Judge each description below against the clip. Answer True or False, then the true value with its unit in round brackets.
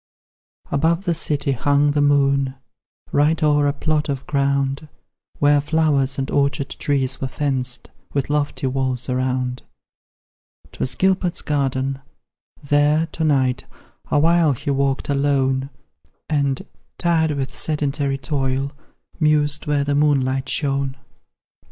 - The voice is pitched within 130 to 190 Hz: True (140 Hz)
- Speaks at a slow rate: True (120 wpm)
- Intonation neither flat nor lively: False (1.7 semitones)